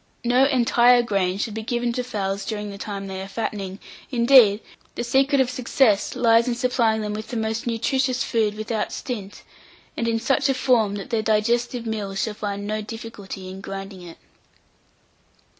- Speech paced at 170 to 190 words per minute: Yes, average, 175 wpm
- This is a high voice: Yes, high, 220 Hz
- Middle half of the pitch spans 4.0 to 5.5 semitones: No, average, 3.1 semitones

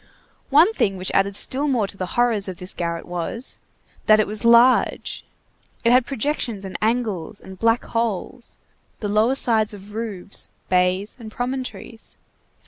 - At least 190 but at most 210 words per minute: No, average, 155 wpm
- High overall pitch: Yes, high, 215 Hz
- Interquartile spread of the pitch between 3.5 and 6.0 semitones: Yes, average, 3.8 semitones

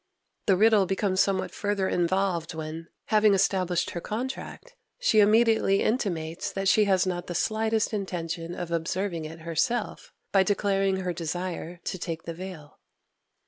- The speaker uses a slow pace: No, average, 145 wpm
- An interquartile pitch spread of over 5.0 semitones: No, average, 3.3 semitones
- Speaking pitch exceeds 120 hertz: Yes, high, 190 Hz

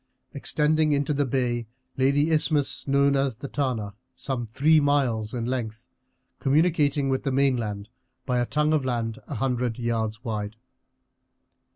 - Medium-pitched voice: No, low, 130 Hz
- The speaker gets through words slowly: No, average, 150 wpm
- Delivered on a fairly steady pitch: No, average, 3.6 semitones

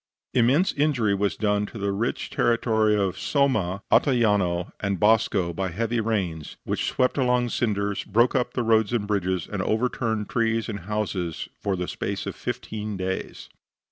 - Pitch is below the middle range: Yes, low, 105 Hz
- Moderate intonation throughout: Yes, average, 3.1 semitones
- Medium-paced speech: Yes, average, 160 wpm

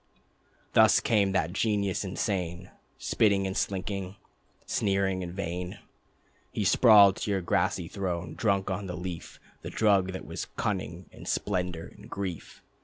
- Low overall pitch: Yes, very low, 95 Hz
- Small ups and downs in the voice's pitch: Yes, narrow, 1.9 semitones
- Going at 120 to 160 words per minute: Yes, average, 140 wpm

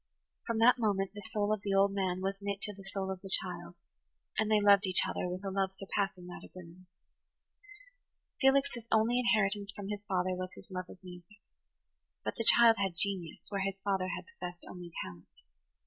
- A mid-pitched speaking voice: No, high, 195 Hz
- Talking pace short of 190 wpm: No, average, 195 wpm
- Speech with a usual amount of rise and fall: No, narrow, 2.2 semitones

